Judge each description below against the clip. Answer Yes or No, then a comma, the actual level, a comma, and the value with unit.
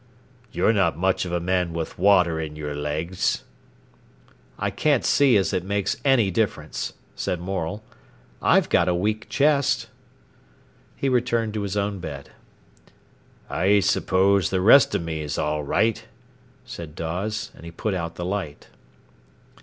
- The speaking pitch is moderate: No, very low, 95 Hz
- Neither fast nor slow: Yes, average, 145 wpm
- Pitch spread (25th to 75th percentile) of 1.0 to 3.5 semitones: No, average, 4.2 semitones